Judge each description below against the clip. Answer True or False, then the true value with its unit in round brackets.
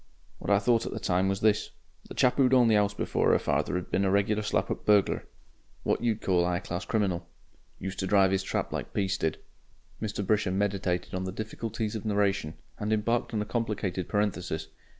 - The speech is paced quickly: True (210 wpm)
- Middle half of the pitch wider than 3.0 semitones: False (2.4 semitones)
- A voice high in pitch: False (100 Hz)